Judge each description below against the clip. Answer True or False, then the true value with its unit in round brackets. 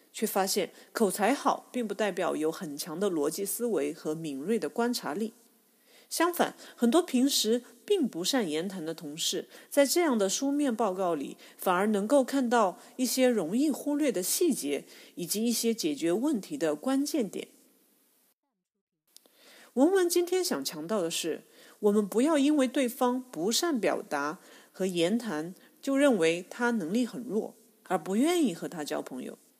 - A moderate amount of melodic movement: False (6.4 semitones)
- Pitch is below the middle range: False (235 Hz)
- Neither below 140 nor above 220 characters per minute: False (235 characters per minute)